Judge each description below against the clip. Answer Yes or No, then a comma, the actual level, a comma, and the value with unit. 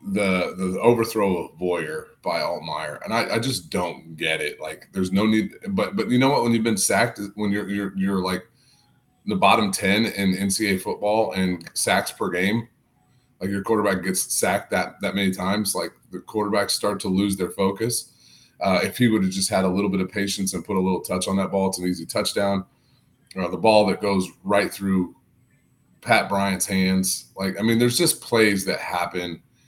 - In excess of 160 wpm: Yes, fast, 205 wpm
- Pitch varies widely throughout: No, narrow, 2.6 semitones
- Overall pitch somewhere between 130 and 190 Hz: No, low, 100 Hz